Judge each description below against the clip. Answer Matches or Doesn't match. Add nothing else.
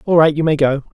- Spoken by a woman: Doesn't match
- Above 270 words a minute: Matches